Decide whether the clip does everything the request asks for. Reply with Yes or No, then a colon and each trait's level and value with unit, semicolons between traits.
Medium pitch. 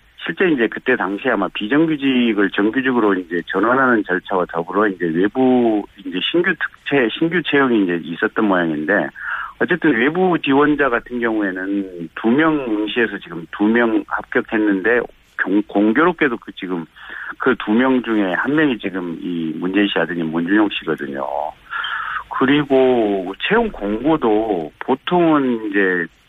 No: low, 105 Hz